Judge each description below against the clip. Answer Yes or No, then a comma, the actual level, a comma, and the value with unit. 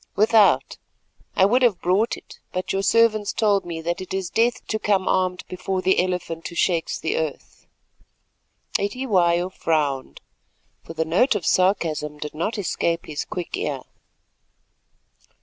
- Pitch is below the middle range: No, medium, 185 Hz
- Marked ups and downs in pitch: No, average, 3.7 semitones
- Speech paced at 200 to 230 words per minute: No, average, 150 wpm